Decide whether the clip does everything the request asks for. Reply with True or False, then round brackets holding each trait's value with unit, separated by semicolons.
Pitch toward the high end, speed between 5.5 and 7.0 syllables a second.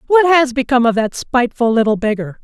True (250 Hz; 6.2 syllables/s)